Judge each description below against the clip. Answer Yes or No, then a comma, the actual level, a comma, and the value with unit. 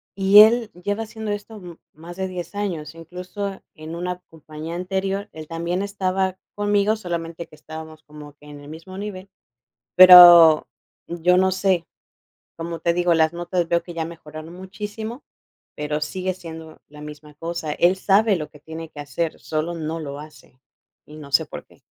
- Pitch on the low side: No, medium, 170 Hz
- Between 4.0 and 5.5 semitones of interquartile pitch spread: No, average, 3.2 semitones